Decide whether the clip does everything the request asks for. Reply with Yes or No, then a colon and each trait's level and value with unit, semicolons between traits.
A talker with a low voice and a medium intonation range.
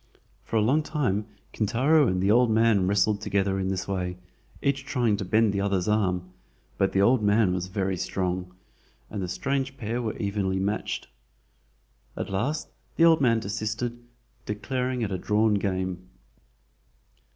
Yes: low, 105 Hz; average, 3.8 semitones